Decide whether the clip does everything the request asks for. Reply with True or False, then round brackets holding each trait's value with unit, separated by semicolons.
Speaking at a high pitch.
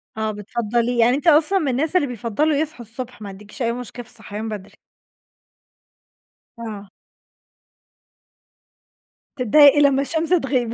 True (245 Hz)